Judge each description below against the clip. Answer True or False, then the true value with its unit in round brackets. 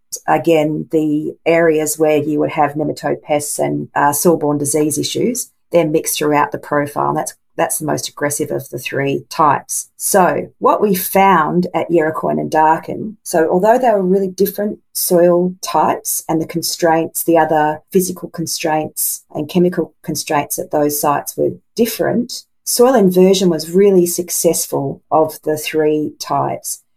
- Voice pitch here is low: False (160 Hz)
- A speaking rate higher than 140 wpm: True (155 wpm)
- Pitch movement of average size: True (3.0 semitones)